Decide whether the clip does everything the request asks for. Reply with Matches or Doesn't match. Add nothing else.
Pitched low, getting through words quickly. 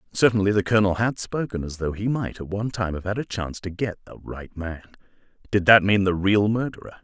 Matches